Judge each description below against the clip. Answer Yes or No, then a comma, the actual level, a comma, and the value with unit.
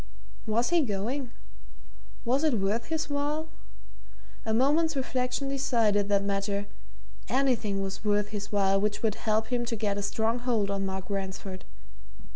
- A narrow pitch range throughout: No, average, 4.4 semitones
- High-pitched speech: Yes, high, 220 Hz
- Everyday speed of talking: Yes, average, 150 wpm